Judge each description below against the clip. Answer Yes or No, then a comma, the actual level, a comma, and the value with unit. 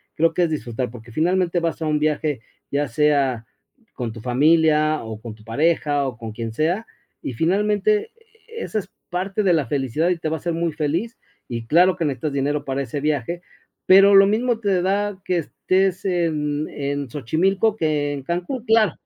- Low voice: No, medium, 155 Hz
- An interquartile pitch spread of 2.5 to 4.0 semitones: No, average, 4.9 semitones